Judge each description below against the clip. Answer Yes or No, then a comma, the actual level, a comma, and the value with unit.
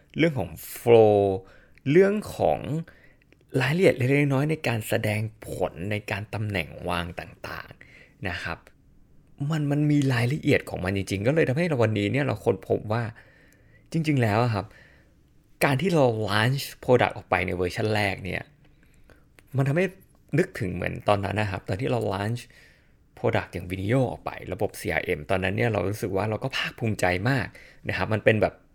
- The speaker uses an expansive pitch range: Yes, wide, 5.7 semitones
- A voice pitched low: Yes, low, 115 Hz